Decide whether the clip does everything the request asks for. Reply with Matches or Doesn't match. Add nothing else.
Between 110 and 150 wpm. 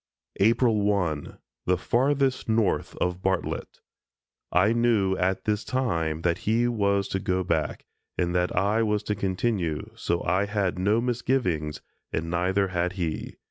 Matches